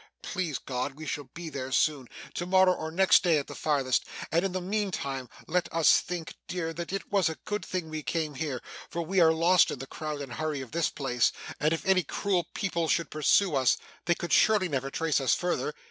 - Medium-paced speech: No, fast, 225 wpm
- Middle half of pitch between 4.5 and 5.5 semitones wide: No, average, 3.9 semitones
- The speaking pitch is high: No, medium, 160 Hz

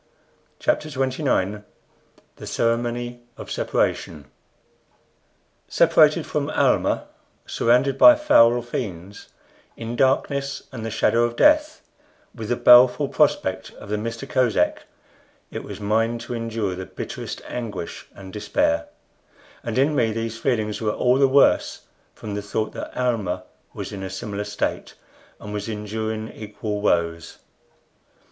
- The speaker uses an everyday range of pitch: Yes, average, 3.2 semitones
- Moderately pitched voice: No, low, 115 Hz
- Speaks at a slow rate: Yes, slow, 130 wpm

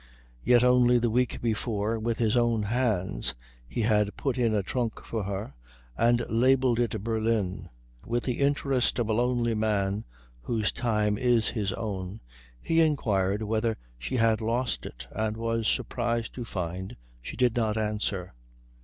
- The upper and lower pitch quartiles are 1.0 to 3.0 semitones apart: Yes, narrow, 2.4 semitones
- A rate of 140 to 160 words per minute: Yes, average, 155 wpm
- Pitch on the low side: Yes, low, 115 Hz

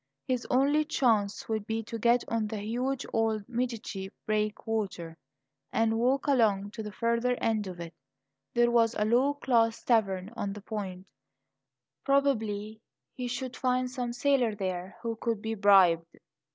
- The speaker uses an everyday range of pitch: Yes, average, 3.2 semitones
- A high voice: Yes, high, 225 Hz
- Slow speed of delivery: No, average, 155 wpm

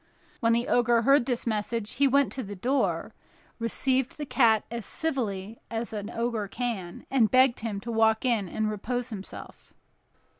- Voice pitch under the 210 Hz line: No, high, 230 Hz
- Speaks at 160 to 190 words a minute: Yes, average, 165 wpm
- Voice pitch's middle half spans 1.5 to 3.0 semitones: Yes, average, 2.7 semitones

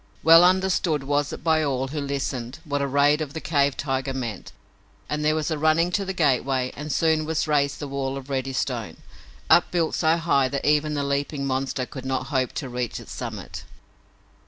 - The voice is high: No, medium, 145 Hz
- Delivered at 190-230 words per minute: Yes, average, 200 wpm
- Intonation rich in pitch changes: No, average, 2.7 semitones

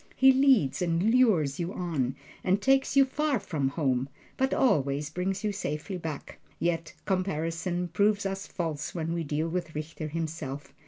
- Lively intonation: No, average, 4.6 semitones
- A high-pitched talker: No, medium, 170 Hz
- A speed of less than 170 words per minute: Yes, average, 160 wpm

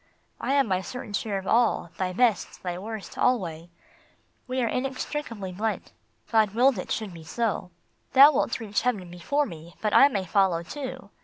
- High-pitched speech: Yes, high, 215 Hz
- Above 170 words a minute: Yes, average, 180 wpm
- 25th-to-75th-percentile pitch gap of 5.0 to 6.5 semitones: Yes, wide, 5.4 semitones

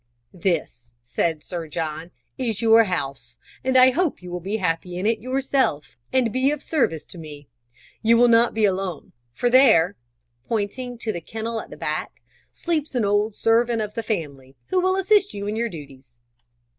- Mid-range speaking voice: No, high, 210 Hz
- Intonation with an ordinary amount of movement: No, wide, 6.9 semitones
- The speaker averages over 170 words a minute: Yes, average, 180 wpm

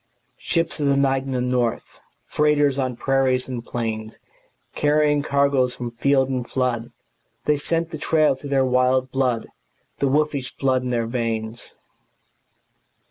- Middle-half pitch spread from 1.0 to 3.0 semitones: Yes, narrow, 2.4 semitones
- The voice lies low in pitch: Yes, low, 130 Hz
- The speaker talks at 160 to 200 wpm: No, average, 150 wpm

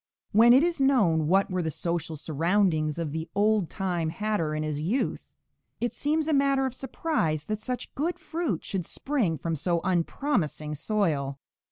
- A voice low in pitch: No, medium, 185 Hz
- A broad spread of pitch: Yes, wide, 8.0 semitones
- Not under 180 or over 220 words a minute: No, average, 170 wpm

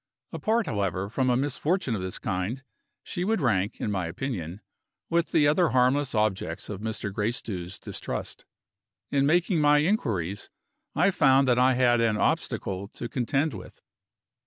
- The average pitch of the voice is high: No, low, 125 Hz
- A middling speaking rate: Yes, average, 155 wpm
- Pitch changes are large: Yes, wide, 6.4 semitones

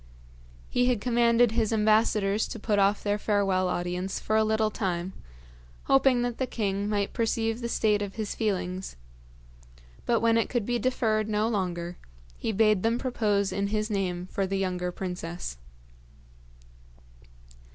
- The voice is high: Yes, high, 210 Hz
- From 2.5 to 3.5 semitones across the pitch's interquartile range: Yes, average, 2.8 semitones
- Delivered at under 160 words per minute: Yes, average, 150 wpm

